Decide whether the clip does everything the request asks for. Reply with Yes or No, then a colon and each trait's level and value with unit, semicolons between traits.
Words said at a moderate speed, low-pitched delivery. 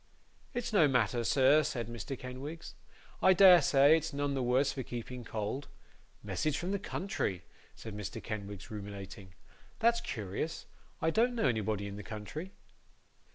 Yes: average, 155 wpm; low, 130 Hz